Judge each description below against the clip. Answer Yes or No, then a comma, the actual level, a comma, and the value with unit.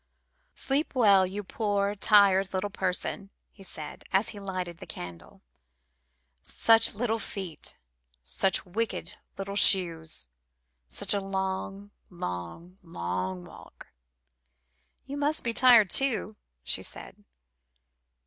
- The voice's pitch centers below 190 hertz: No, high, 195 Hz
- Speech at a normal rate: No, slow, 110 wpm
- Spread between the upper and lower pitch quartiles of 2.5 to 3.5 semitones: Yes, average, 3.2 semitones